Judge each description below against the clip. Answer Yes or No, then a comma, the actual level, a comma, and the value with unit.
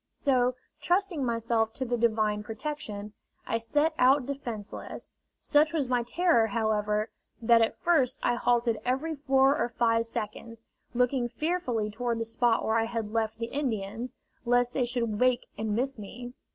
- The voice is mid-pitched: No, high, 240 Hz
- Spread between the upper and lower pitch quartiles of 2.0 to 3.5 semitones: Yes, average, 2.9 semitones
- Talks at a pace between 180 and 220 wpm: No, average, 160 wpm